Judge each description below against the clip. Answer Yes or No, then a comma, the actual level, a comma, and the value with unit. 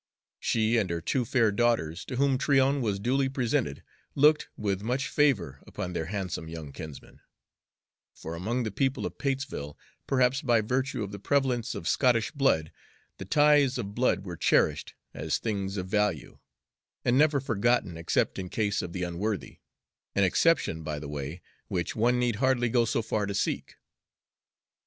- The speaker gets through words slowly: No, average, 165 wpm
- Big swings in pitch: Yes, wide, 6.0 semitones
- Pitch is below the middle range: Yes, low, 110 Hz